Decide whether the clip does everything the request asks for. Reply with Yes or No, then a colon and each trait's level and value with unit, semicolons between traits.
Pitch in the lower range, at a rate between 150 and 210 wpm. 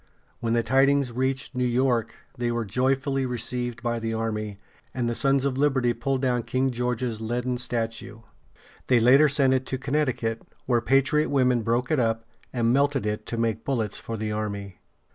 Yes: low, 125 Hz; average, 180 wpm